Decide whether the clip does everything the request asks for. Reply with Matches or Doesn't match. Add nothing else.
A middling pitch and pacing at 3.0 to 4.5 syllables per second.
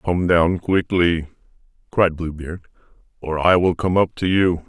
Doesn't match